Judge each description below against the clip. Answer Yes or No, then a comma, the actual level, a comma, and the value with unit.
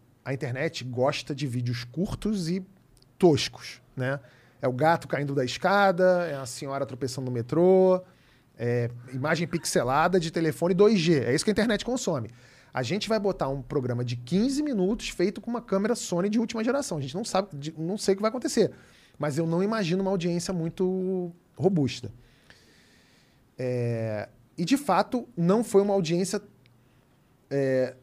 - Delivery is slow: No, average, 165 wpm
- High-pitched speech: No, medium, 165 Hz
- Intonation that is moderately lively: No, wide, 6.9 semitones